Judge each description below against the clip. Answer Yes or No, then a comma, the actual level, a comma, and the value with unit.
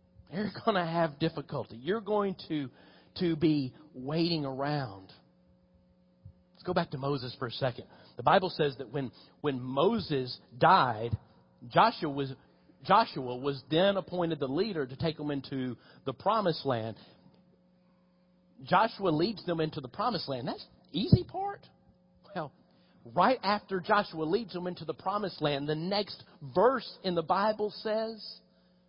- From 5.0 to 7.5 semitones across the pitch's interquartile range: Yes, average, 5.3 semitones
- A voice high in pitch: No, medium, 160 Hz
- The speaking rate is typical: Yes, average, 145 wpm